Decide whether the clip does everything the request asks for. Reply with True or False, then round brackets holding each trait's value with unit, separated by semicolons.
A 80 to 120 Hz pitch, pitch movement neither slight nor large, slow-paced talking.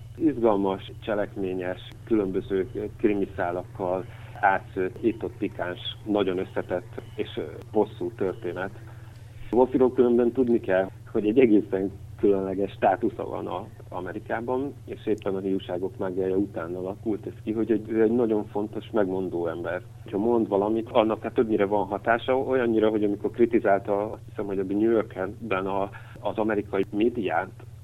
False (105 Hz; 3.0 semitones; 130 wpm)